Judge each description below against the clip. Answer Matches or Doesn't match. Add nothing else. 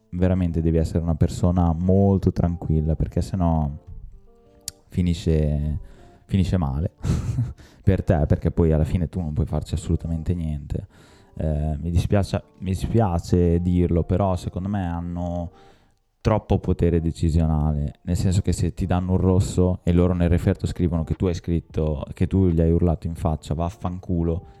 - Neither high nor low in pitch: Doesn't match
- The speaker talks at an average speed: Matches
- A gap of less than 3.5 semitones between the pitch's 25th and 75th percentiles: Matches